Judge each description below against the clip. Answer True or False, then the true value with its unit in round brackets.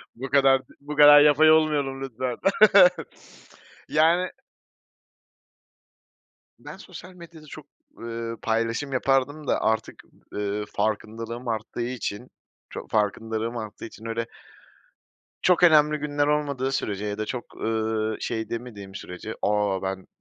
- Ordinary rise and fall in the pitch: True (4.9 semitones)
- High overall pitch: False (120 Hz)